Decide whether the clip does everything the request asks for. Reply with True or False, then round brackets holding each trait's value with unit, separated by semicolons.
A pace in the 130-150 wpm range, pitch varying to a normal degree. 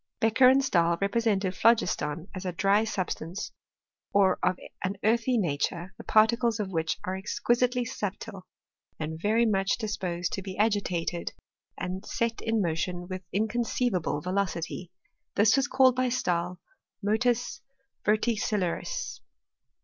True (135 wpm; 4.1 semitones)